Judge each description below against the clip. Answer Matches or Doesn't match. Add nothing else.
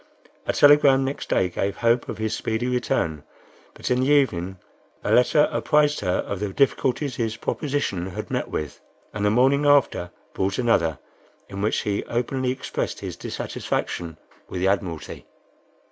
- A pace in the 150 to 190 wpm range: Matches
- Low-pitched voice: Matches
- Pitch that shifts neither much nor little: Doesn't match